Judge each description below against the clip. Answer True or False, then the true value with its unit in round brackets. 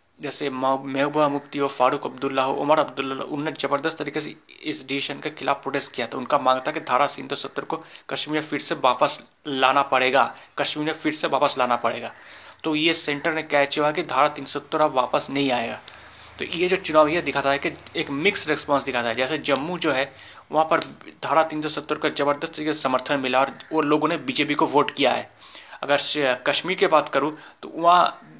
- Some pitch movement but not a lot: False (2.1 semitones)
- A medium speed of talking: False (205 wpm)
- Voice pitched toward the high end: False (145 Hz)